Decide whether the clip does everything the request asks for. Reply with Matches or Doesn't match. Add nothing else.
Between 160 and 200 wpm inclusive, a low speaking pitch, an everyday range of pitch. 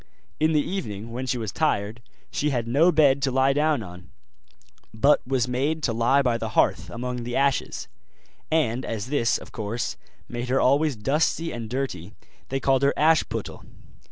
Matches